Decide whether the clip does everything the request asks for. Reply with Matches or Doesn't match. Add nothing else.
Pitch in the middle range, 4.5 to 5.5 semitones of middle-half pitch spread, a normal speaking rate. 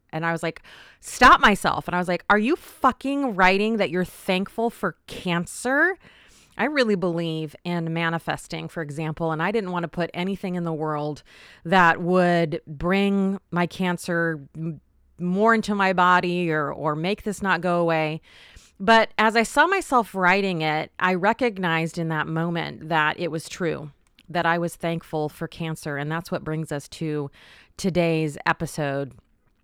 Doesn't match